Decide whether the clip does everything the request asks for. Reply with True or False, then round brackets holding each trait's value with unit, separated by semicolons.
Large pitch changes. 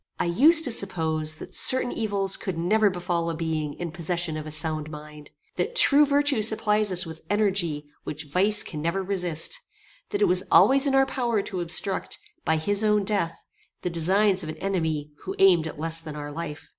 False (4.8 semitones)